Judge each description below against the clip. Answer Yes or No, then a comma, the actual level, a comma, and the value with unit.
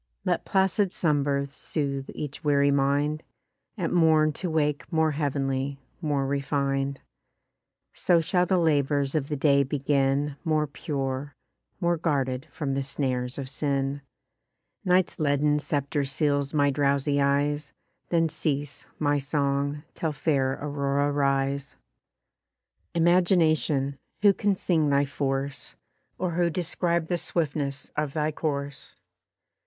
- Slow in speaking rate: Yes, slow, 125 wpm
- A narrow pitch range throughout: Yes, narrow, 2.1 semitones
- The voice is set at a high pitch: No, medium, 145 Hz